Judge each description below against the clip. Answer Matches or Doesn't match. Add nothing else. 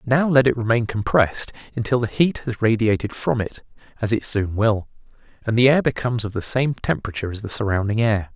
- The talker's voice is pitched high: Doesn't match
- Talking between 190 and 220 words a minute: Matches